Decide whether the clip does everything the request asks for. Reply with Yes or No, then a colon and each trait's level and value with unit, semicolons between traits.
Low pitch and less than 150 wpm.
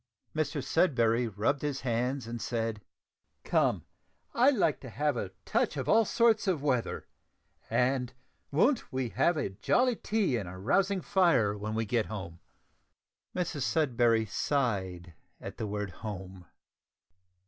Yes: low, 125 Hz; average, 140 wpm